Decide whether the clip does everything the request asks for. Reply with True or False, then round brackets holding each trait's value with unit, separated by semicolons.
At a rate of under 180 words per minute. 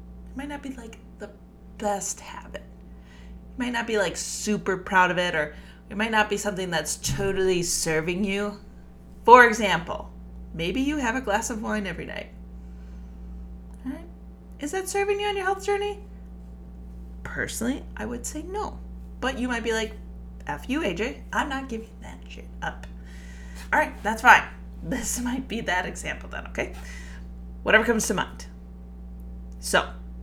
True (165 wpm)